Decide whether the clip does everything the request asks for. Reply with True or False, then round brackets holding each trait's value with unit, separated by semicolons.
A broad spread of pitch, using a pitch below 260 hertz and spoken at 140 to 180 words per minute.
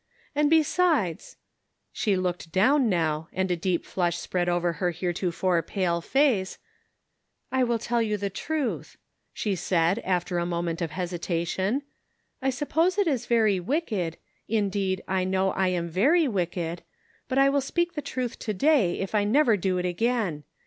True (6.3 semitones; 190 Hz; 175 wpm)